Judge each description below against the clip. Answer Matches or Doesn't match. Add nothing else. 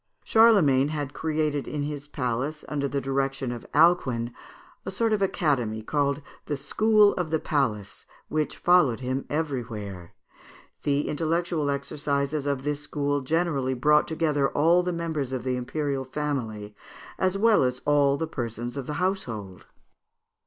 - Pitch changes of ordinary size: Matches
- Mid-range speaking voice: Matches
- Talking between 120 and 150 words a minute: Matches